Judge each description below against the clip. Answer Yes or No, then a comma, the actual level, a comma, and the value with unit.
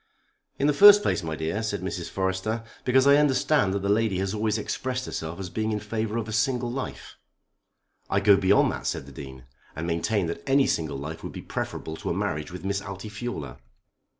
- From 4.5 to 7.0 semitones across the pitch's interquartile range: Yes, average, 5.3 semitones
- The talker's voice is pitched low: Yes, low, 105 Hz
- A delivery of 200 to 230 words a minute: Yes, fast, 205 wpm